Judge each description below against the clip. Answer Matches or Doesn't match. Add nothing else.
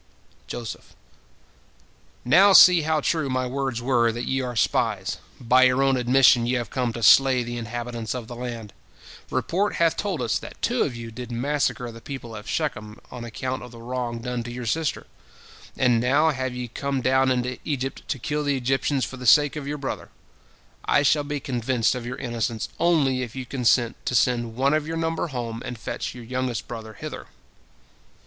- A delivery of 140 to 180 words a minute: Doesn't match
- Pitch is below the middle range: Matches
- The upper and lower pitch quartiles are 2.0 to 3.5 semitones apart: Matches